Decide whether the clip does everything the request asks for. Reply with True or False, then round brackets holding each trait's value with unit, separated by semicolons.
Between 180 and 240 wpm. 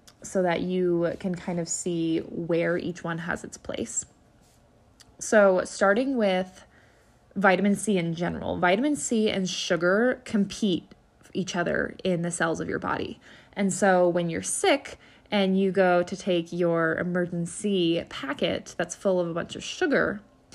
False (155 wpm)